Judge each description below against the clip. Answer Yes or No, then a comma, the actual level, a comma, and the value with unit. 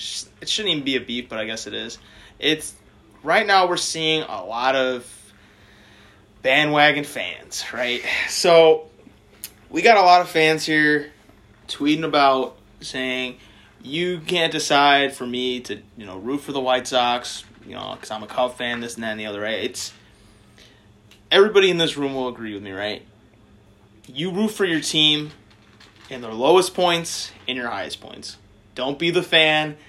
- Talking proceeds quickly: No, average, 175 wpm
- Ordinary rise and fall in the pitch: No, wide, 6.5 semitones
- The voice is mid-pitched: No, low, 125 Hz